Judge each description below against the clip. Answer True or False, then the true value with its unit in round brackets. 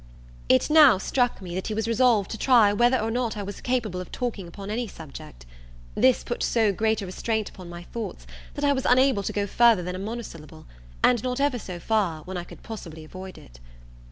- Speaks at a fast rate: True (215 wpm)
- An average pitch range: True (4.7 semitones)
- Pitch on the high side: True (215 Hz)